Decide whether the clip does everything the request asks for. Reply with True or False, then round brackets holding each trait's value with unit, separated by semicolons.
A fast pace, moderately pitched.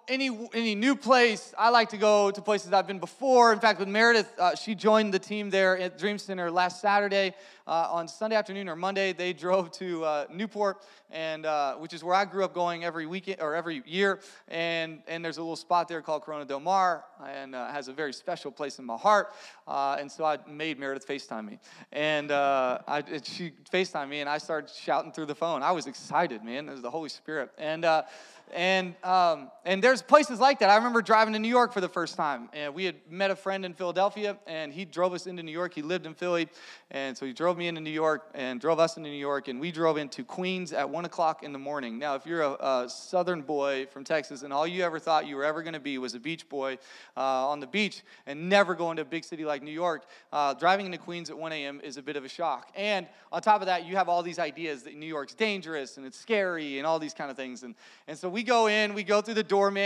True (255 wpm; 170 Hz)